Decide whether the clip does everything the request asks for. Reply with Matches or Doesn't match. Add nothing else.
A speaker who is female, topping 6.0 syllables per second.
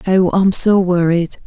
Doesn't match